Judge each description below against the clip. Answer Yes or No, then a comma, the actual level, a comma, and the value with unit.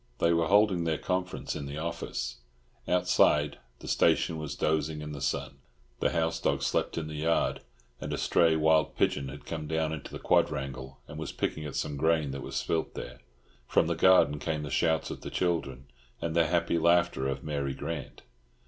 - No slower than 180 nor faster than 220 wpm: Yes, average, 195 wpm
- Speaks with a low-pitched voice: Yes, very low, 80 Hz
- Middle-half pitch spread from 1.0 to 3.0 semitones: Yes, average, 2.7 semitones